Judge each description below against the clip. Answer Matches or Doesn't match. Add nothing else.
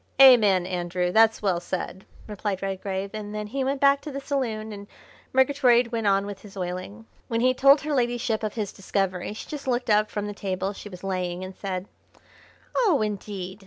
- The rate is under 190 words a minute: Doesn't match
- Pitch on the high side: Matches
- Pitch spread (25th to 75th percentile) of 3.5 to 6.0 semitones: Matches